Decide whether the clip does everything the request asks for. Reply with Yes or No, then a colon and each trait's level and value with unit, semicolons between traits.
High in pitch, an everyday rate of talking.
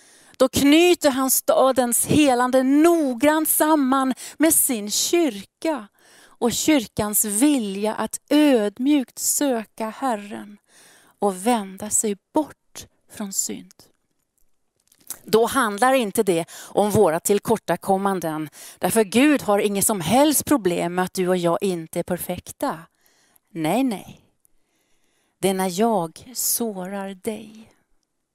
No: high, 225 Hz; slow, 110 wpm